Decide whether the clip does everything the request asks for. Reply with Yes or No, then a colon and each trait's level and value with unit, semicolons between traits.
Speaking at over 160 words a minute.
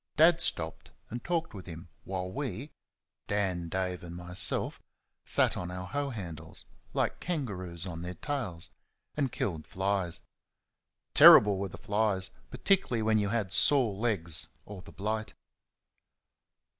No: slow, 135 wpm